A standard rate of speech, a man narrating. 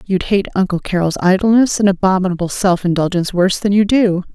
No: average, 180 wpm; female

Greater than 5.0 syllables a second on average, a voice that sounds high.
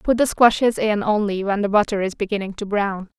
Yes: 5.6 syllables/s; high, 210 Hz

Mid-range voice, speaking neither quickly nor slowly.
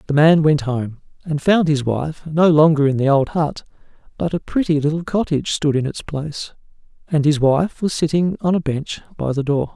No: medium, 155 Hz; fast, 210 wpm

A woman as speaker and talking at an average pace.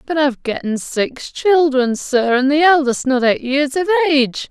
Yes: female; average, 185 wpm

